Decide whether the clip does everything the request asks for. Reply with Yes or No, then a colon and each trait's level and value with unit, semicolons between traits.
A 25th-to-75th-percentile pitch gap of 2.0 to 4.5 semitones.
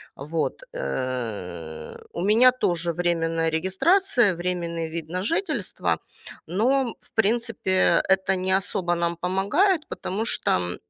No: average, 5.3 semitones